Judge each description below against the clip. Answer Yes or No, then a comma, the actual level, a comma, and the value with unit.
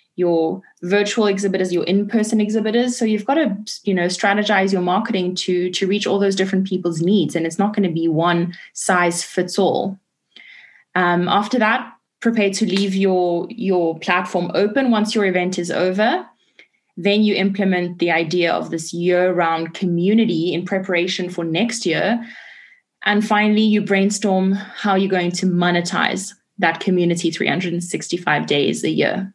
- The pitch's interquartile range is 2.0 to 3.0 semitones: Yes, average, 2.7 semitones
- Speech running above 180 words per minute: No, average, 155 wpm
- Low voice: No, high, 190 Hz